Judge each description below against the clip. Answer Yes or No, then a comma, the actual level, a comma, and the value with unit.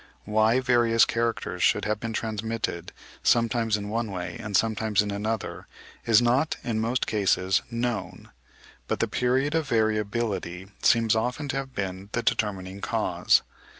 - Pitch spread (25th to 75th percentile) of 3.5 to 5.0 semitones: No, narrow, 2.5 semitones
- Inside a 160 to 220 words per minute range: No, average, 150 wpm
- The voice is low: Yes, low, 110 Hz